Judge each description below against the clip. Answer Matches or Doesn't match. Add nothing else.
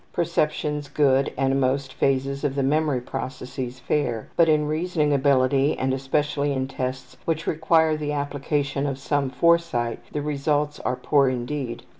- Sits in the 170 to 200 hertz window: Doesn't match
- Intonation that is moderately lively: Doesn't match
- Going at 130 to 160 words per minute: Matches